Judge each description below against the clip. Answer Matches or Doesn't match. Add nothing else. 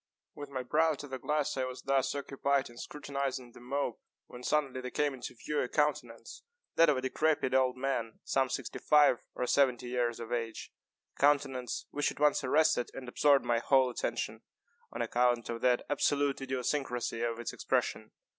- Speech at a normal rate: Matches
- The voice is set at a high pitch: Doesn't match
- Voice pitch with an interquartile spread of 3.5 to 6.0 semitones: Doesn't match